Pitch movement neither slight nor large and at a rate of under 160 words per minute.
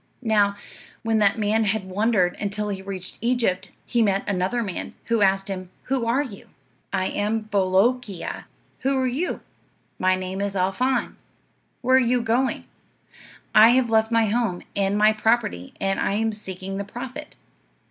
No: average, 3.3 semitones; average, 165 wpm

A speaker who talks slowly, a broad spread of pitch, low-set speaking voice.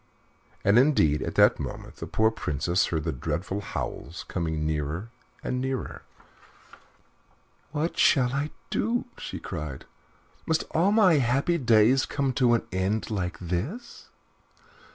Yes: slow, 130 wpm; wide, 8.1 semitones; low, 110 Hz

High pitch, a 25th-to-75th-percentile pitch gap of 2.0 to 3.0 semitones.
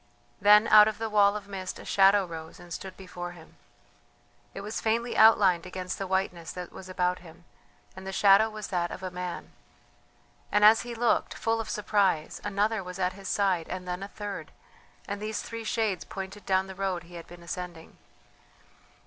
Yes: high, 195 Hz; narrow, 2.6 semitones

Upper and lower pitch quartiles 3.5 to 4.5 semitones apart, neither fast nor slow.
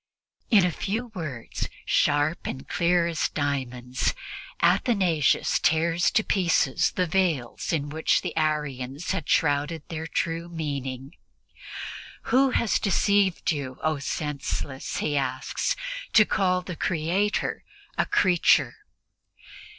No: average, 4.2 semitones; slow, 115 wpm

